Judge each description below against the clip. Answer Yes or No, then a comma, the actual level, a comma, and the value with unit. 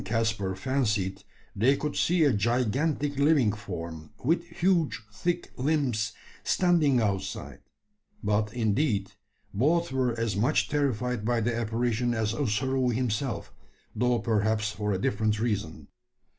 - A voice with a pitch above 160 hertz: No, low, 115 Hz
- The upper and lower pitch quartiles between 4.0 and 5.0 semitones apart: Yes, average, 4.6 semitones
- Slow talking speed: Yes, slow, 130 wpm